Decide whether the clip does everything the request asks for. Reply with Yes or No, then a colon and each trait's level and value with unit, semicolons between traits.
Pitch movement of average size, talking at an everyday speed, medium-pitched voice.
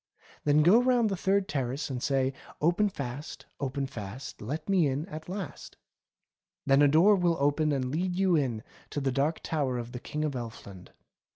Yes: average, 4.9 semitones; average, 185 wpm; medium, 145 Hz